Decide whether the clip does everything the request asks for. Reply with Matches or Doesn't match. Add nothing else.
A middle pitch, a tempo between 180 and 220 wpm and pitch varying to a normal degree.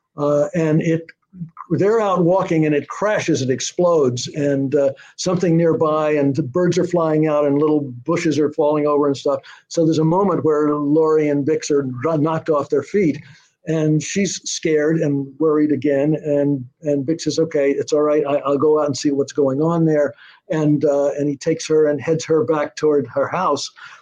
Doesn't match